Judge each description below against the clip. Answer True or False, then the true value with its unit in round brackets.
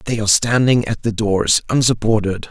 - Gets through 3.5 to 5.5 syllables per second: True (5.3 syllables/s)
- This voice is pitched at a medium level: False (110 Hz)